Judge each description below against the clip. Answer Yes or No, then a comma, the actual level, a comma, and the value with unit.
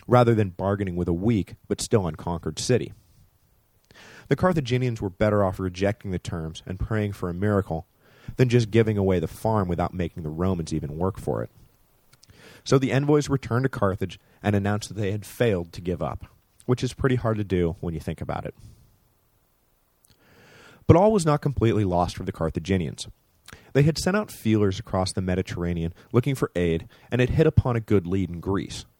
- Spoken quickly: No, average, 190 wpm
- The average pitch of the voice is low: Yes, low, 105 Hz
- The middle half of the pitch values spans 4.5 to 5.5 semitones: Yes, average, 4.8 semitones